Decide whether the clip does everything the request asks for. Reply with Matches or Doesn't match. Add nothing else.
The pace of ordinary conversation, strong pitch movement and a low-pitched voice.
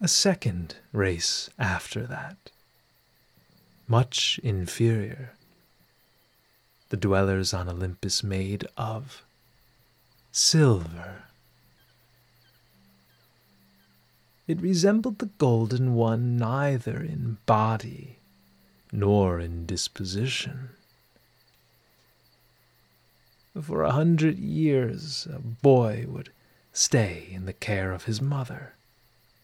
Doesn't match